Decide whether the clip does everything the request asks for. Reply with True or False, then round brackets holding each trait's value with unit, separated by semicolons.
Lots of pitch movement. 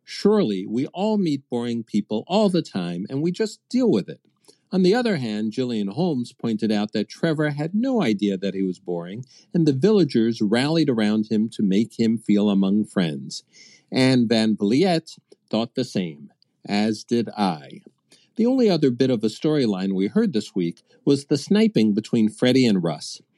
True (7.8 semitones)